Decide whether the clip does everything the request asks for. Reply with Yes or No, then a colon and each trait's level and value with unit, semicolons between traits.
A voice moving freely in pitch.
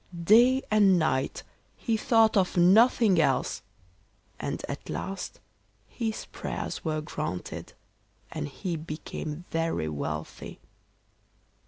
Yes: wide, 6.1 semitones